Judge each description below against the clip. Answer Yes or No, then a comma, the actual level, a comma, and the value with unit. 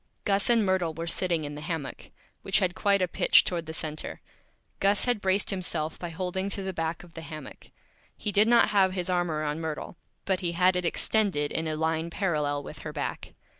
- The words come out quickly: Yes, fast, 210 wpm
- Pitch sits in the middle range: Yes, medium, 175 Hz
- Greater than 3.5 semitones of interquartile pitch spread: No, average, 3.1 semitones